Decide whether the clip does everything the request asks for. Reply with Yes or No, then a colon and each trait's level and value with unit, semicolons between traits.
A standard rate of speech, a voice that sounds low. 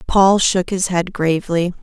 No: average, 165 wpm; medium, 180 Hz